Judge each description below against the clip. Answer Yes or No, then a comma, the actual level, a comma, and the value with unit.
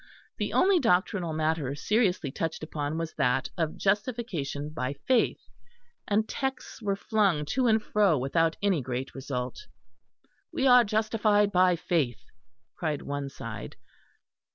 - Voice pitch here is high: No, medium, 170 Hz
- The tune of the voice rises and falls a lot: Yes, wide, 6.8 semitones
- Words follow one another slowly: Yes, slow, 130 wpm